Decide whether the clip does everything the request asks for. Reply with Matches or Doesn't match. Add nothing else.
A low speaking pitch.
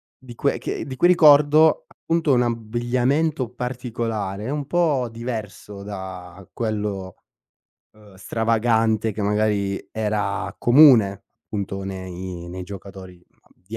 Matches